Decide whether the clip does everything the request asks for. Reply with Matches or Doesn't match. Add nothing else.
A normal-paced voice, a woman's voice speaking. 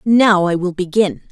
Matches